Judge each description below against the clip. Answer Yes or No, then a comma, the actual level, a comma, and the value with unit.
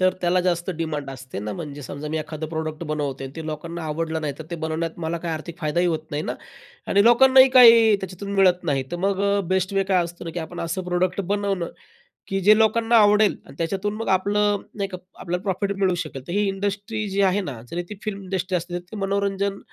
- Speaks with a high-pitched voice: No, medium, 180 Hz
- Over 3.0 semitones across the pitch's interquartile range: Yes, average, 3.9 semitones